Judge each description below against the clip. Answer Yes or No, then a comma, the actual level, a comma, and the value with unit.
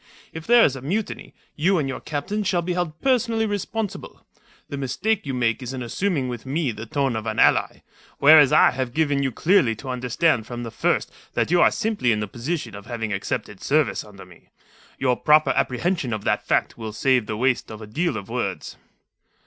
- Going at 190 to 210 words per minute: Yes, fast, 205 wpm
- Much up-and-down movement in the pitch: Yes, wide, 6.5 semitones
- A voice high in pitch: No, low, 135 Hz